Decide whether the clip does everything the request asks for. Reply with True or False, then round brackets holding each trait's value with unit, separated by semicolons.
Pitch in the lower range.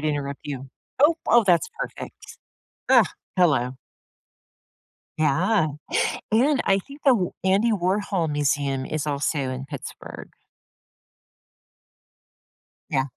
False (160 Hz)